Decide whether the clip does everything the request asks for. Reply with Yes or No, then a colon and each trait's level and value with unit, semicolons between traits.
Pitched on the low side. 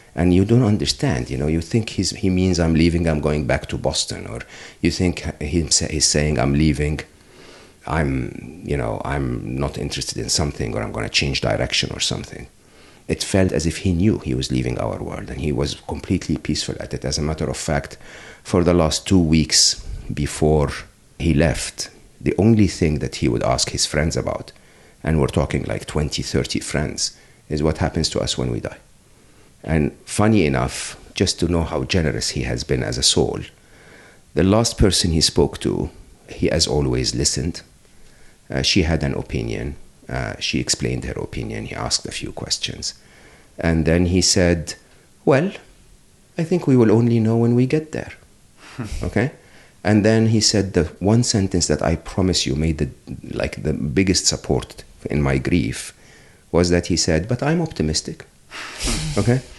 Yes: very low, 85 Hz